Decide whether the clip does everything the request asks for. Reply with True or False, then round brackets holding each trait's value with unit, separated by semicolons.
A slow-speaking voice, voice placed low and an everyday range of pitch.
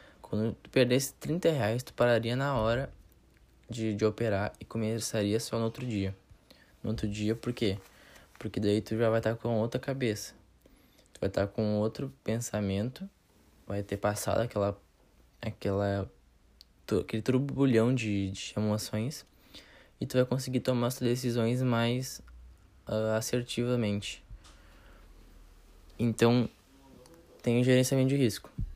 False (140 wpm; 110 Hz; 3.5 semitones)